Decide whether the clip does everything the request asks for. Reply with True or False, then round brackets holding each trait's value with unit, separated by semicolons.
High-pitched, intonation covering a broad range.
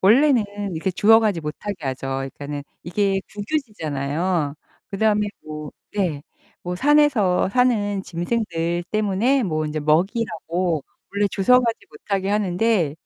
False (195 Hz; 5.0 semitones)